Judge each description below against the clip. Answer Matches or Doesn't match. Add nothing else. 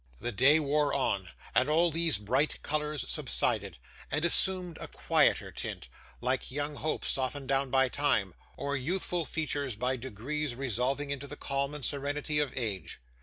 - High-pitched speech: Doesn't match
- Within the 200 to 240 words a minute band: Doesn't match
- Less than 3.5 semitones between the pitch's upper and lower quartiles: Matches